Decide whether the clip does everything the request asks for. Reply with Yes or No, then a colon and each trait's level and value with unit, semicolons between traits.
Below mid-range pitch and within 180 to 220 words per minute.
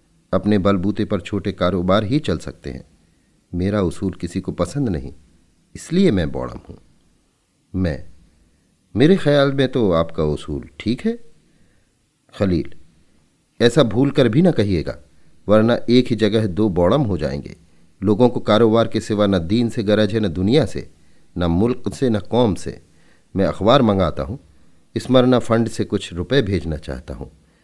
No: low, 100 Hz; average, 160 wpm